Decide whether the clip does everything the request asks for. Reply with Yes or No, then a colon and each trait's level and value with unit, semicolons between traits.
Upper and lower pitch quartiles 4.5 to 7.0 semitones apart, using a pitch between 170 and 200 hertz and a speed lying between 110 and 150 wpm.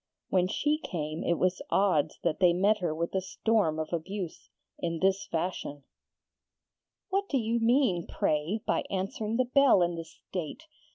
No: average, 4.8 semitones; medium, 185 Hz; average, 165 wpm